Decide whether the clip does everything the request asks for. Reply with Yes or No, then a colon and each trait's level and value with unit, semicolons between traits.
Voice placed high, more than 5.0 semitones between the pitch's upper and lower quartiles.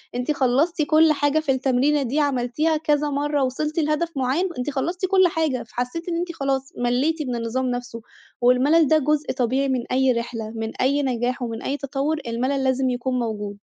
No: very high, 270 Hz; average, 3.5 semitones